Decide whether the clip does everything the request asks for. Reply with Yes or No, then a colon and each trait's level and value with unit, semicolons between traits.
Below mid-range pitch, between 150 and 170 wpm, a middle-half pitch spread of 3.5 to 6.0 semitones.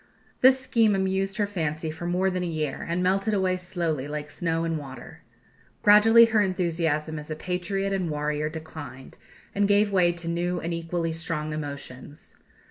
No: medium, 170 Hz; average, 165 wpm; average, 3.8 semitones